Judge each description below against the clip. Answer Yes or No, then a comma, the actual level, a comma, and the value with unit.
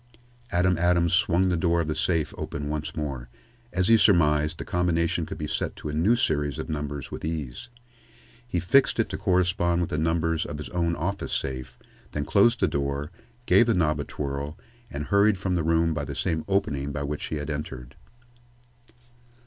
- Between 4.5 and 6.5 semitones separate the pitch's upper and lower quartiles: No, average, 3.4 semitones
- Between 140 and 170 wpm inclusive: No, average, 195 wpm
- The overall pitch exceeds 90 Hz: No, very low, 80 Hz